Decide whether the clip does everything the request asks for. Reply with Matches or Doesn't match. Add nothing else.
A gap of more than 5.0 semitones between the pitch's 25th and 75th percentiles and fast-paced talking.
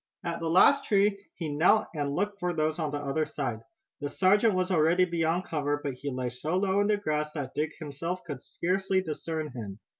Doesn't match